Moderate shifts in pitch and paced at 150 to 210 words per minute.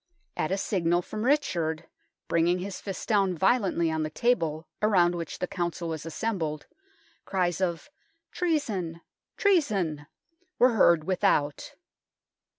No: average, 5.0 semitones; slow, 135 wpm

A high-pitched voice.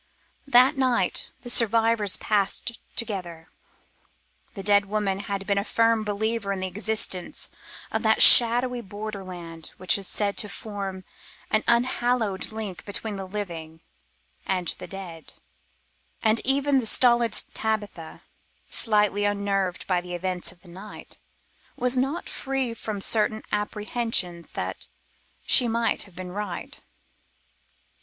Yes: high, 205 Hz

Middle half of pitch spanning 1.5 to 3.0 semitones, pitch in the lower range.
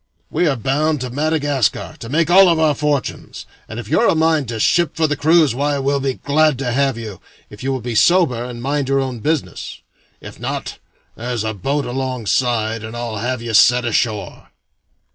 No: average, 4.0 semitones; low, 130 Hz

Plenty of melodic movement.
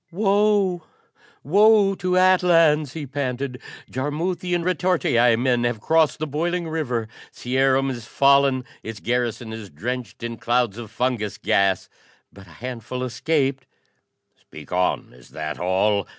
Yes: wide, 5.9 semitones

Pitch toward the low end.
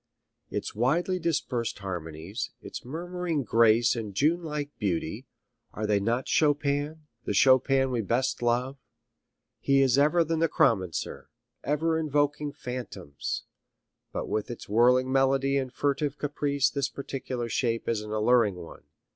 Yes: low, 130 Hz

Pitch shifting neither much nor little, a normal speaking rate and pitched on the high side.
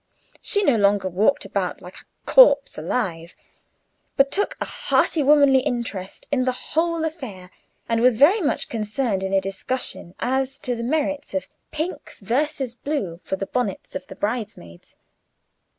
No: wide, 6.6 semitones; average, 155 wpm; very high, 250 Hz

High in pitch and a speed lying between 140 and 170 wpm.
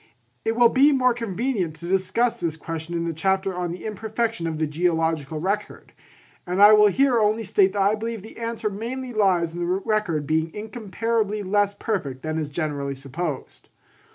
No: high, 195 Hz; average, 180 wpm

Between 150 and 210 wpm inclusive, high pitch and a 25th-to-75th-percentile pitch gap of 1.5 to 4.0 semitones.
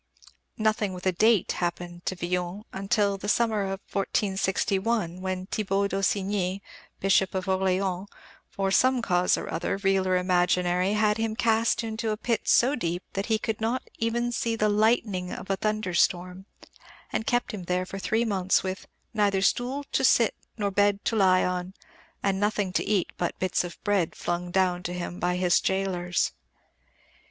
Yes: average, 170 wpm; high, 195 Hz; average, 2.8 semitones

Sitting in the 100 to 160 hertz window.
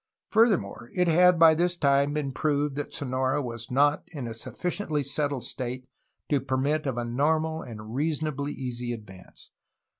Yes: medium, 140 Hz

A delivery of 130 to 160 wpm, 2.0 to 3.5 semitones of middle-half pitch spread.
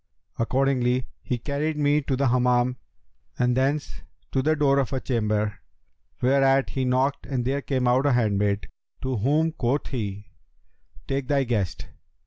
Yes: average, 150 wpm; narrow, 2.4 semitones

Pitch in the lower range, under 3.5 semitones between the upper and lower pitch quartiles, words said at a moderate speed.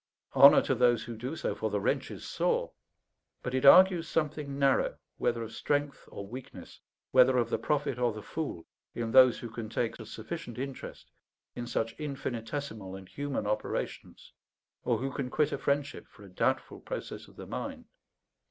No: low, 125 Hz; average, 3.8 semitones; average, 180 wpm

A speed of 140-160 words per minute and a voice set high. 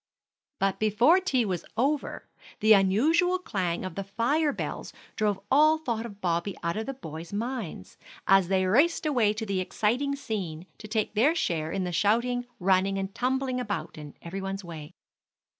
No: average, 175 wpm; high, 210 Hz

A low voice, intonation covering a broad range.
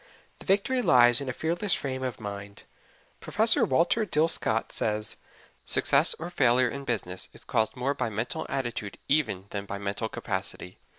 Yes: low, 125 Hz; wide, 6.3 semitones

